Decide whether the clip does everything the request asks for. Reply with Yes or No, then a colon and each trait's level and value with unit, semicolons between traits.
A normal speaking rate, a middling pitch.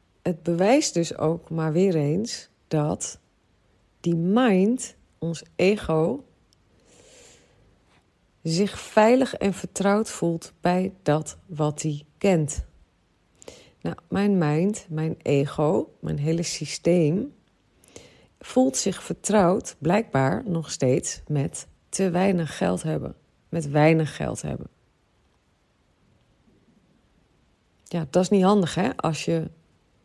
No: slow, 105 wpm; medium, 165 Hz